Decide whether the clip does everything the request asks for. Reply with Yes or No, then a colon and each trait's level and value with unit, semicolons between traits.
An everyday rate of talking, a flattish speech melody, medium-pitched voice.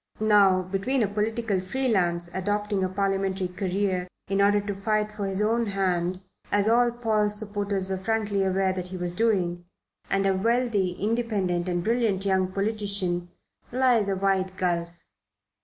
No: average, 155 wpm; narrow, 2.3 semitones; high, 195 Hz